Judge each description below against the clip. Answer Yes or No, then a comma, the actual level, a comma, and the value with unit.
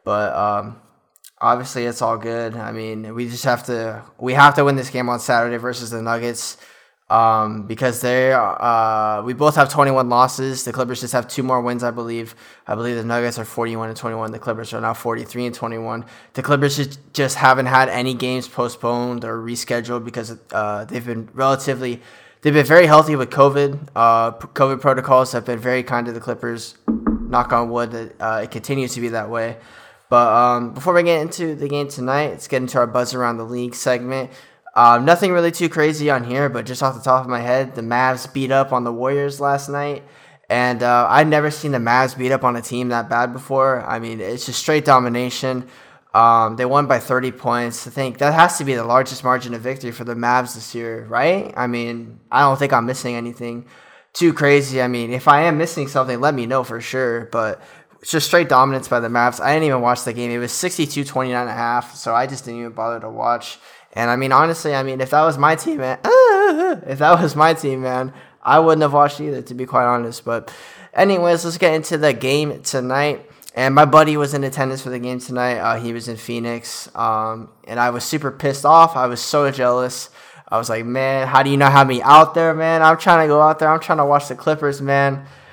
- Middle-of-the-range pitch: No, low, 125 Hz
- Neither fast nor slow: No, fast, 225 wpm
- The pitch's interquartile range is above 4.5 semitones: No, average, 3.0 semitones